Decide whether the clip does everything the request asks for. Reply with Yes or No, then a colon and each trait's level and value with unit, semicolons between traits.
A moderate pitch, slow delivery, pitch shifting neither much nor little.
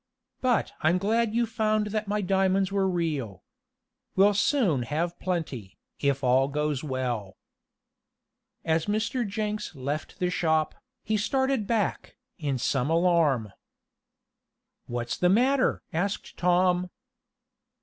No: medium, 180 Hz; slow, 120 wpm; wide, 6.6 semitones